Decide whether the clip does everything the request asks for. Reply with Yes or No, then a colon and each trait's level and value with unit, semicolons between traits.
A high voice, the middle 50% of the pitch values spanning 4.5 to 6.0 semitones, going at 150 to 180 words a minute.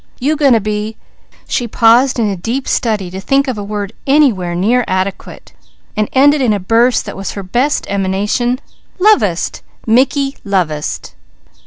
Yes: high, 225 Hz; average, 4.8 semitones; average, 160 wpm